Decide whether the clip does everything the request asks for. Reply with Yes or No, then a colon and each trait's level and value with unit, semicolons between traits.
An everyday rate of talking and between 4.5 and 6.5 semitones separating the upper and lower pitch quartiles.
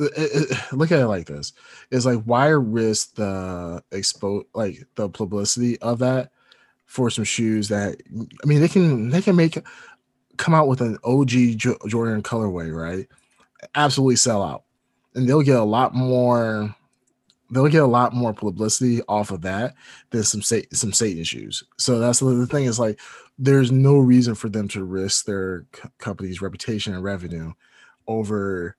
No: average, 165 wpm; average, 3.9 semitones